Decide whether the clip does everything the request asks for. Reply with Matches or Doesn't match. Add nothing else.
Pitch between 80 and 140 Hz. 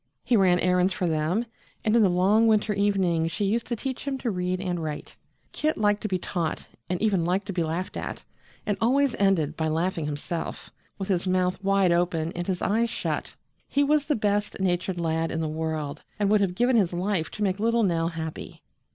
Doesn't match